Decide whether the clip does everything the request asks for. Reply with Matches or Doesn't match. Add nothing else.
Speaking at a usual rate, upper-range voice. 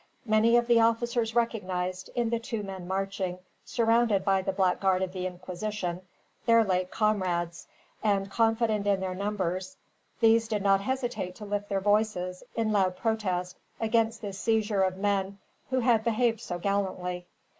Matches